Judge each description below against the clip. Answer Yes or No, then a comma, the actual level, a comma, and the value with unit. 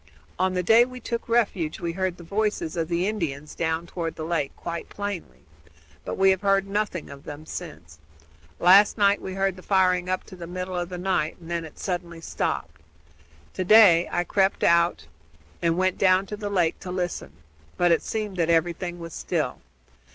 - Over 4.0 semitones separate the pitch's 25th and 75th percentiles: No, narrow, 2.5 semitones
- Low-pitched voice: No, medium, 180 Hz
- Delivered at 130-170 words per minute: No, average, 195 wpm